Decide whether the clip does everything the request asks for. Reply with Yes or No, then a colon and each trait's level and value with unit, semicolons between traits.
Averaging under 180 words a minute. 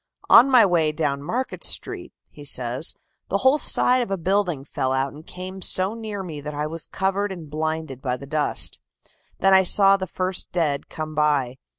No: average, 195 wpm